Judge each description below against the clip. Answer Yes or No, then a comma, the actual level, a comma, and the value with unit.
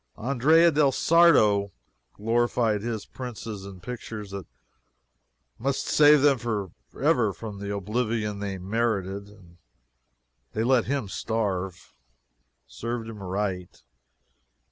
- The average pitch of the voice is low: Yes, low, 110 Hz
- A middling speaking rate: No, slow, 110 wpm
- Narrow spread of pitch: No, average, 3.8 semitones